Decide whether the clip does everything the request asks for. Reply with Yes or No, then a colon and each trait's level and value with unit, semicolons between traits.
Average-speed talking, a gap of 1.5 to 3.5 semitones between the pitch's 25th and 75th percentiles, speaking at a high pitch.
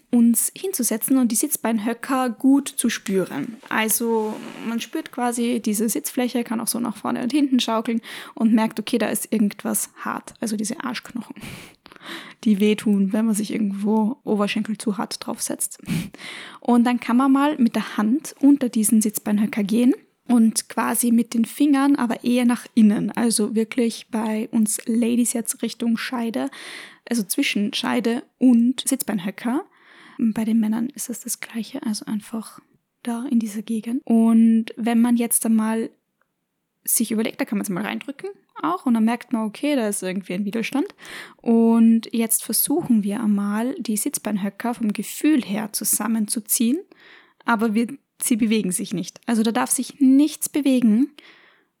Yes: average, 160 wpm; narrow, 2.6 semitones; high, 235 Hz